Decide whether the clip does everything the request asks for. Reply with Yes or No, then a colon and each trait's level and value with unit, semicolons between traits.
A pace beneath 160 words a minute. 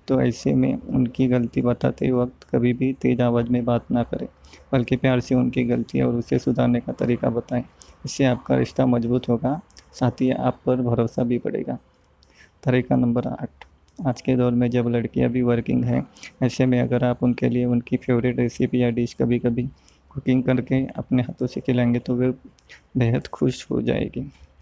No: average, 185 wpm